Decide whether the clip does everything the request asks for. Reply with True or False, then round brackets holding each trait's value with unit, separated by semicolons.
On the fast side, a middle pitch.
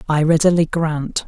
False (140 wpm; 160 Hz)